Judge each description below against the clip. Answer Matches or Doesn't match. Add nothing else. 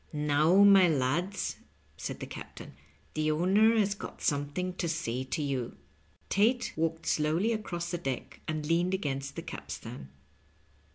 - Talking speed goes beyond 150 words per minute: Doesn't match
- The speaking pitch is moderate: Matches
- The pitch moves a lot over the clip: Doesn't match